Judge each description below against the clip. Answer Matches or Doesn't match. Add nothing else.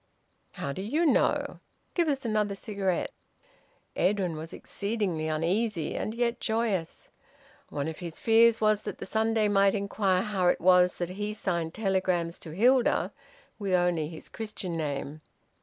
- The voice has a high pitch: Matches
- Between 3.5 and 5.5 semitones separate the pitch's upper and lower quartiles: Matches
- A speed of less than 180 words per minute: Matches